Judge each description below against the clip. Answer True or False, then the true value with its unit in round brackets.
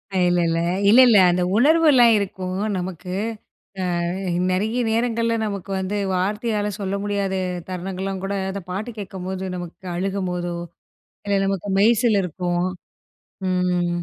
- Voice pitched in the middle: False (195 Hz)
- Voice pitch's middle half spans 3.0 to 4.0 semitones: False (2.5 semitones)